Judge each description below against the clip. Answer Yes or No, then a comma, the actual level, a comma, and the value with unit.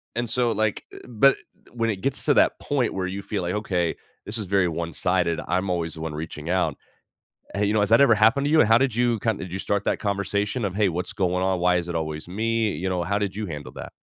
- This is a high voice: No, low, 100 Hz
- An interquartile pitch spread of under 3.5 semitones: No, average, 3.9 semitones